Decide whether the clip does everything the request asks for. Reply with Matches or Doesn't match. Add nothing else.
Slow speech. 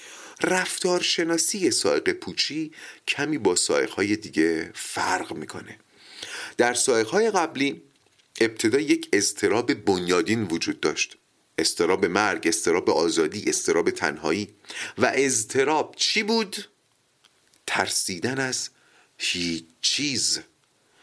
Matches